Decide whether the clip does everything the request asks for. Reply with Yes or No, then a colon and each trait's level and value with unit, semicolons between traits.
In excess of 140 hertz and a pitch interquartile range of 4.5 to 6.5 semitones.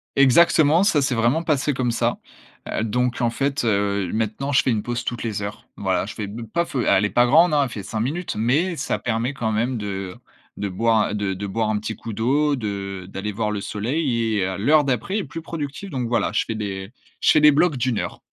No: low, 115 Hz; average, 5.1 semitones